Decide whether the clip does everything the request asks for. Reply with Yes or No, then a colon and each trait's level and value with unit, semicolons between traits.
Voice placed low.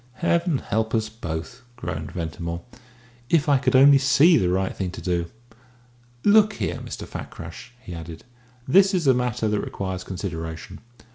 Yes: low, 110 Hz